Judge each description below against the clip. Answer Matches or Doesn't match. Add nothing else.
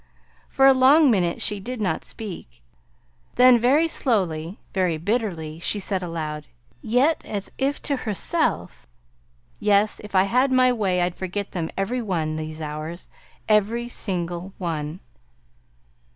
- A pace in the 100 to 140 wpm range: Matches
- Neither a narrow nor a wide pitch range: Doesn't match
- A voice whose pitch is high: Matches